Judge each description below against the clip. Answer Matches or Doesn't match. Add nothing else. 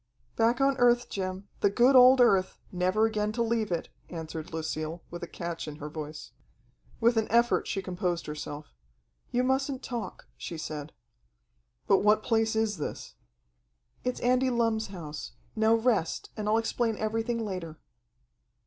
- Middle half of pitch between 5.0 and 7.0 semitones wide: Matches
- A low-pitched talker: Doesn't match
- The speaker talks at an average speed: Matches